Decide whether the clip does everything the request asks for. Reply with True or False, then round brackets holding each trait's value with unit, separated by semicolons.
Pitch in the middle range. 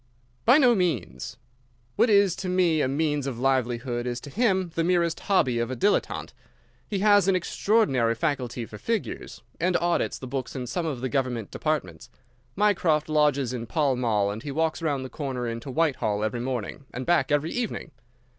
True (145 Hz)